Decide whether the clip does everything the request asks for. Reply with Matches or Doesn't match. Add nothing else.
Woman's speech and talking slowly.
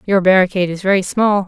Doesn't match